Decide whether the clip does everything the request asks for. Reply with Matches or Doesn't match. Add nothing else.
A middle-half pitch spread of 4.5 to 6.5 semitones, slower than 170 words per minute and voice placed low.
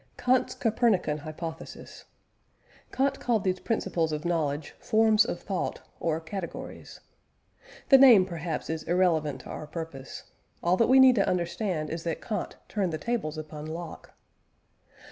Doesn't match